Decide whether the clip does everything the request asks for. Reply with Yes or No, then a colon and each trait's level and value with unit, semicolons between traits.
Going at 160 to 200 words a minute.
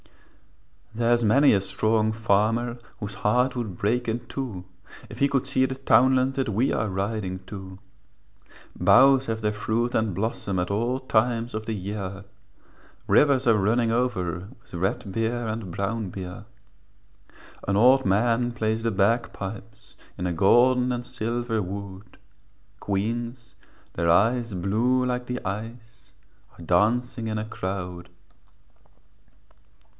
No: slow, 135 wpm